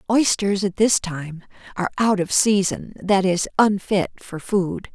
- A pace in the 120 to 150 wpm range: Yes, average, 145 wpm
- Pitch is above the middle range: Yes, high, 195 Hz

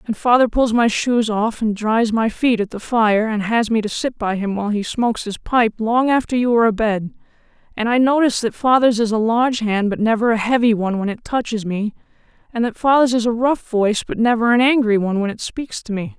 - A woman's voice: Yes, female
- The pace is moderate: No, fast, 240 wpm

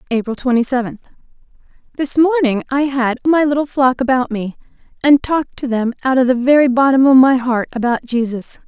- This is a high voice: Yes, very high, 260 Hz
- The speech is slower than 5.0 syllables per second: No, 5.6 syllables/s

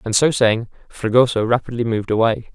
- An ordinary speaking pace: Yes, average, 165 wpm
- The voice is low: Yes, low, 115 Hz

